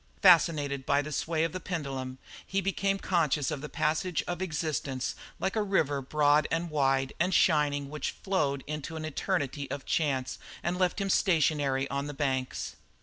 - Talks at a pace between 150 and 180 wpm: Yes, average, 175 wpm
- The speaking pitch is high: No, medium, 150 Hz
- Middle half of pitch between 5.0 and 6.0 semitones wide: No, average, 3.7 semitones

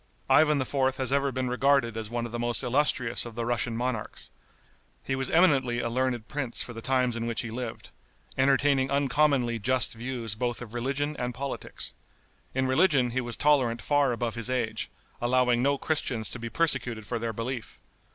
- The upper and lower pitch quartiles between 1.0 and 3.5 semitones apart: Yes, narrow, 2.5 semitones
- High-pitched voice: No, low, 125 Hz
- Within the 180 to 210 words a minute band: Yes, average, 185 wpm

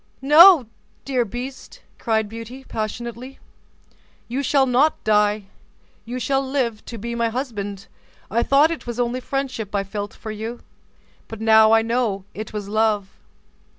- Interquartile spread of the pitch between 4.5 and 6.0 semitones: No, average, 3.2 semitones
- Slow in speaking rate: No, average, 150 wpm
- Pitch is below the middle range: No, high, 230 Hz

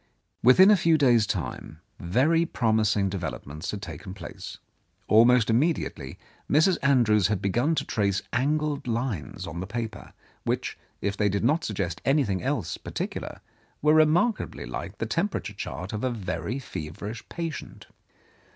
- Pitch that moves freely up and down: Yes, wide, 6.6 semitones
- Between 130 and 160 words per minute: Yes, average, 150 wpm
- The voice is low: Yes, low, 115 Hz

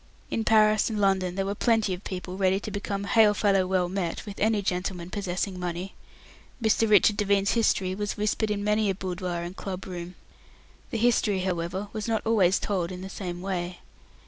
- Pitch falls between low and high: No, high, 195 Hz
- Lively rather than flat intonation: No, narrow, 2.5 semitones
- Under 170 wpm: No, average, 190 wpm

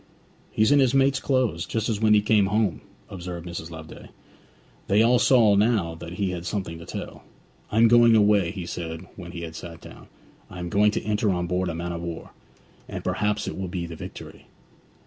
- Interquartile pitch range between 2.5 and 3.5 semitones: No, average, 4.1 semitones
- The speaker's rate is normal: No, fast, 210 wpm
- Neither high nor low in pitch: No, very low, 95 Hz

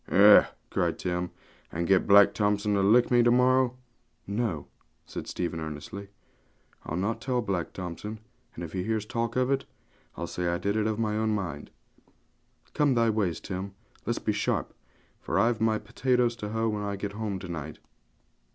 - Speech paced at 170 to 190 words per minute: Yes, average, 180 wpm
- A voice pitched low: Yes, low, 105 Hz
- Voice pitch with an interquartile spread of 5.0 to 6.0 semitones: No, average, 3.9 semitones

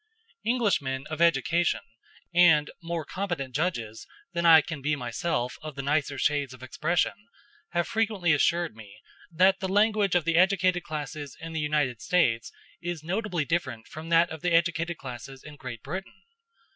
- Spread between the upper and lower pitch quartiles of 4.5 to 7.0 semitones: No, average, 4.0 semitones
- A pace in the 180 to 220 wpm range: No, average, 160 wpm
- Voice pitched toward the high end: No, medium, 160 Hz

